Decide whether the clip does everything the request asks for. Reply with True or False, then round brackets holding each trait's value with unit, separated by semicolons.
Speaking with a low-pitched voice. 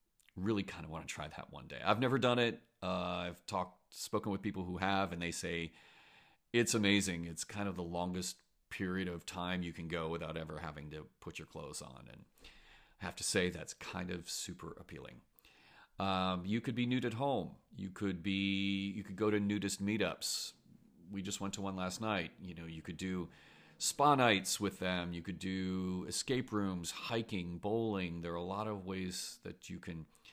True (95 Hz)